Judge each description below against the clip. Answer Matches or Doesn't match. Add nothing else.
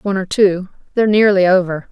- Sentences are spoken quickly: Doesn't match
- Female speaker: Matches